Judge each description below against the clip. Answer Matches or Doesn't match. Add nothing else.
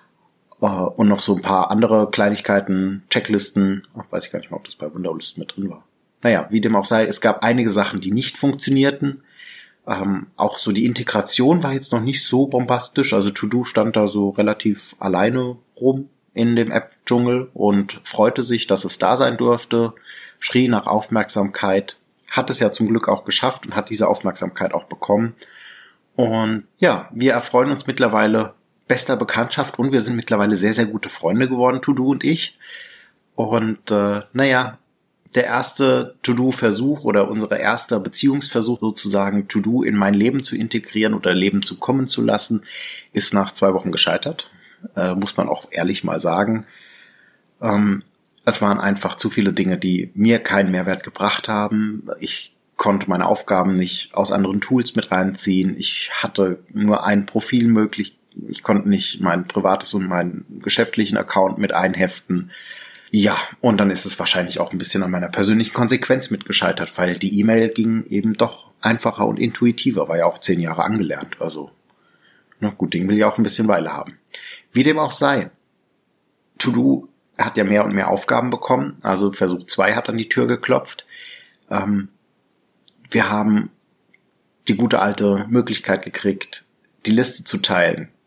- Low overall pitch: Matches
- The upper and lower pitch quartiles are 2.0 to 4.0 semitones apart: Matches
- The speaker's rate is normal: Matches